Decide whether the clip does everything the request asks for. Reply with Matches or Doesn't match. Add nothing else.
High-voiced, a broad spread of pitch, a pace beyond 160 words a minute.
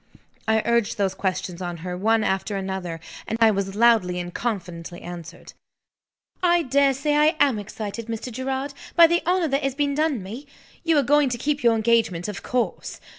Matches